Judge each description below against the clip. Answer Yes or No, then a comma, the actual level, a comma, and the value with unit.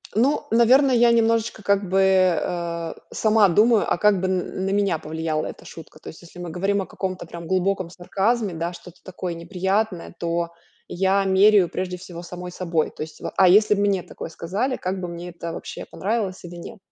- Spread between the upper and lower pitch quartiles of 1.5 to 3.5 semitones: Yes, average, 3.0 semitones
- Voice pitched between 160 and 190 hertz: Yes, medium, 185 Hz